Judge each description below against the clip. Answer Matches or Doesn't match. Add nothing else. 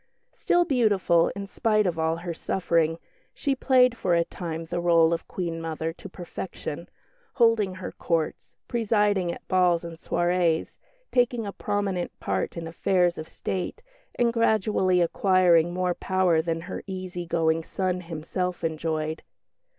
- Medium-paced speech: Matches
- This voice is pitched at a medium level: Matches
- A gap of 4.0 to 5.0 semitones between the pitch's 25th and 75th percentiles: Doesn't match